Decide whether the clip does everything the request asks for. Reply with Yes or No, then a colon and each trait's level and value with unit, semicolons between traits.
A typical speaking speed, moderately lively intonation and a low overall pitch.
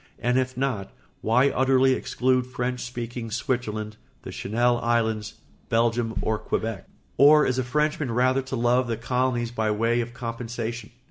No: average, 150 wpm; narrow, 1.9 semitones; low, 120 Hz